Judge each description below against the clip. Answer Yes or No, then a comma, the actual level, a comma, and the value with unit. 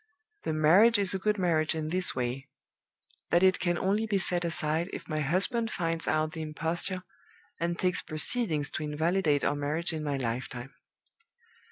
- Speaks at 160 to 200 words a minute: Yes, average, 170 wpm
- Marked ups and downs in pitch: No, average, 3.5 semitones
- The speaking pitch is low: No, medium, 165 Hz